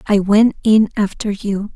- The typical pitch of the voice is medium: No, high, 205 Hz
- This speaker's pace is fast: No, average, 170 wpm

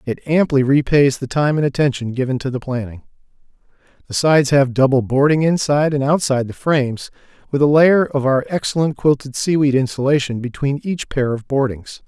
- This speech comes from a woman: No, male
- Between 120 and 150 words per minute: No, average, 175 wpm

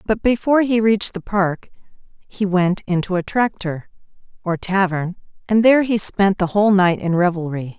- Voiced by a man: No, female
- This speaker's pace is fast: No, average, 170 wpm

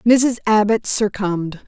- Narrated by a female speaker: Yes, female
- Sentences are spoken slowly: Yes, slow, 110 wpm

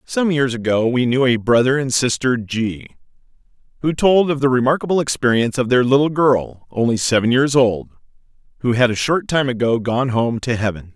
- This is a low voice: Yes, low, 125 Hz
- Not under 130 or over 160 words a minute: No, average, 185 wpm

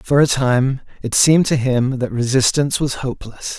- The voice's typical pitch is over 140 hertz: No, low, 130 Hz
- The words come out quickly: No, average, 185 wpm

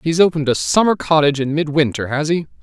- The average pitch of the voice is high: No, medium, 150 Hz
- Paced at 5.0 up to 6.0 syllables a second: No, 6.5 syllables/s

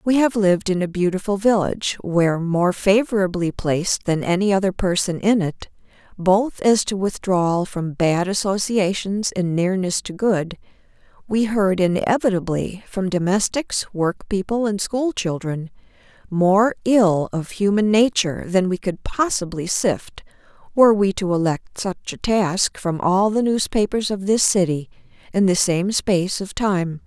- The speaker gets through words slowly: No, average, 150 wpm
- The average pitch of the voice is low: No, high, 195 Hz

